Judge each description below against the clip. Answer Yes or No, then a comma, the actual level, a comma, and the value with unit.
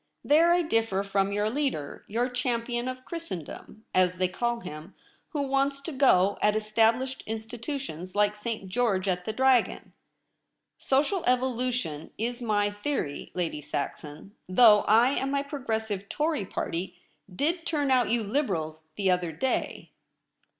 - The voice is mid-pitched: No, high, 225 Hz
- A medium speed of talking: Yes, average, 150 wpm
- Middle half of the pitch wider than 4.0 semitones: Yes, wide, 5.4 semitones